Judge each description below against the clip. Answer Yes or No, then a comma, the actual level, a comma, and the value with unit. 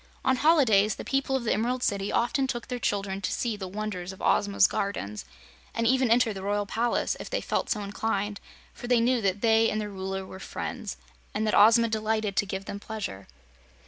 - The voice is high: Yes, high, 215 Hz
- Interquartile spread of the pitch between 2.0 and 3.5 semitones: Yes, average, 3.0 semitones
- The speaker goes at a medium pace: No, fast, 210 wpm